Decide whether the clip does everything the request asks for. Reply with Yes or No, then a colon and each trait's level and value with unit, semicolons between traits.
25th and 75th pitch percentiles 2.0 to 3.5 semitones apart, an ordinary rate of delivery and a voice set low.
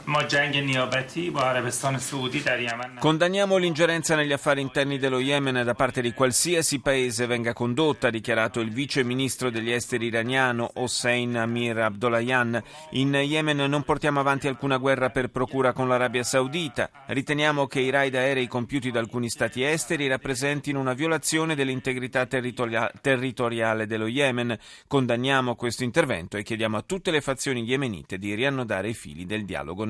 Yes: average, 2.7 semitones; average, 145 wpm; low, 130 Hz